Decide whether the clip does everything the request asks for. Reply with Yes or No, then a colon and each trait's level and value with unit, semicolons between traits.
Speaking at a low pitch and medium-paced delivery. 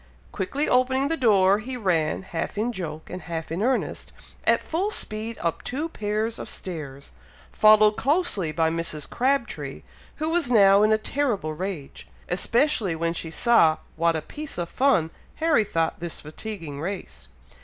No: high, 205 Hz; average, 160 wpm